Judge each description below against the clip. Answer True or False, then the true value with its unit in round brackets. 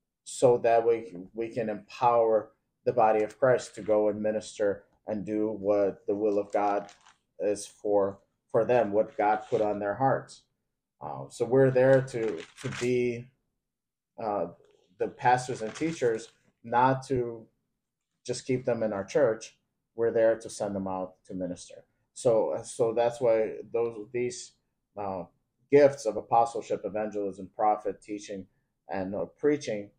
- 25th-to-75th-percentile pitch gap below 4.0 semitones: True (3.1 semitones)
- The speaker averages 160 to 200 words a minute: False (150 wpm)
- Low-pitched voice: True (110 Hz)